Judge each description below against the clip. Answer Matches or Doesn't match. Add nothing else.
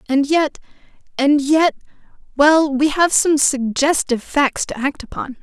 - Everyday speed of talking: Doesn't match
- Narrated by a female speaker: Matches